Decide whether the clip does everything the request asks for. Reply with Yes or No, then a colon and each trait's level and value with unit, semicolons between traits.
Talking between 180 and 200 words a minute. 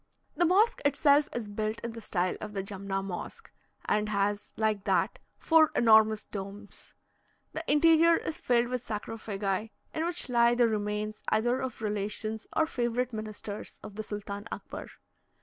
No: average, 155 wpm